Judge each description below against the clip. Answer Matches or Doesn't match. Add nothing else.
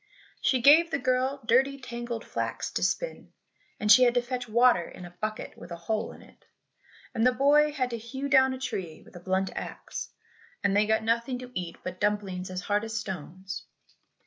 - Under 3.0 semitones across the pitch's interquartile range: Doesn't match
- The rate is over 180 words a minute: Matches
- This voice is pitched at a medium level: Doesn't match